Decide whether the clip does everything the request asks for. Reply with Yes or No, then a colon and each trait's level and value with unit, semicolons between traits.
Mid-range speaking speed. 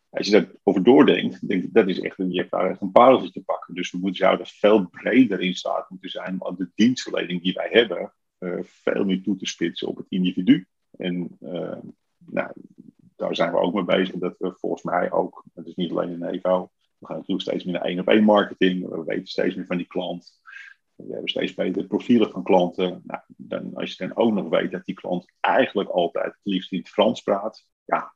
No: fast, 225 wpm